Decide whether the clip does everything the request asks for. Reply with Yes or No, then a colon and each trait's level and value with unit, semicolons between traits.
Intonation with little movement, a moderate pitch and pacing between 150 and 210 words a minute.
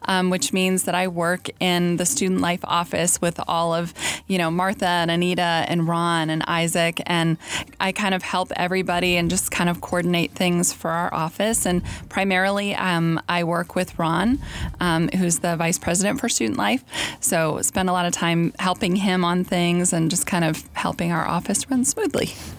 Yes: narrow, 1.6 semitones; medium, 175 Hz; average, 190 wpm